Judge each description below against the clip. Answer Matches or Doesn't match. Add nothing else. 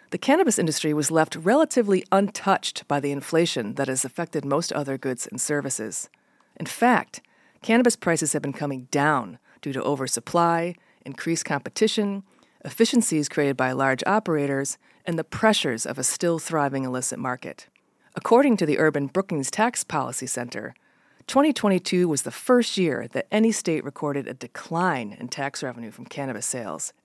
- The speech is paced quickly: Doesn't match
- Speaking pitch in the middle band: Matches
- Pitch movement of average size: Doesn't match